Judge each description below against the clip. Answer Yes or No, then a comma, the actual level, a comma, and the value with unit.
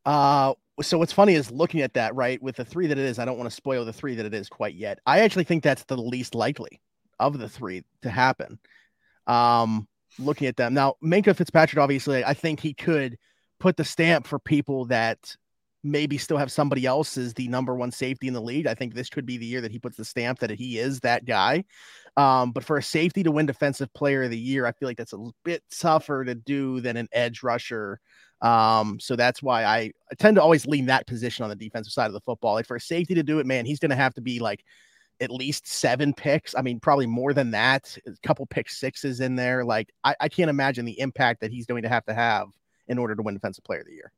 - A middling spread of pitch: Yes, average, 3.5 semitones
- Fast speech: Yes, fast, 250 wpm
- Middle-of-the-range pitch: No, low, 130 Hz